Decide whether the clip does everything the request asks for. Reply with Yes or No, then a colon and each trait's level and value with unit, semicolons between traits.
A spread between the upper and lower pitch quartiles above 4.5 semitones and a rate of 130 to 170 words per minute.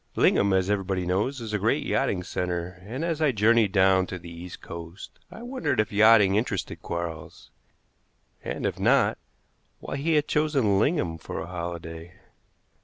Yes: average, 5.0 semitones; average, 165 wpm